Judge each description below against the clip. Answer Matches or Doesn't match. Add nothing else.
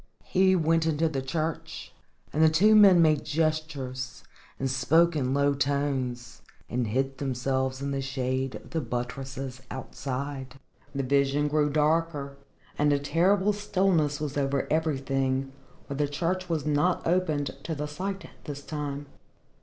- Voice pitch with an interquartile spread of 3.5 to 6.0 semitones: Doesn't match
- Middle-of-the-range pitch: Matches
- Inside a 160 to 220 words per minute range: Doesn't match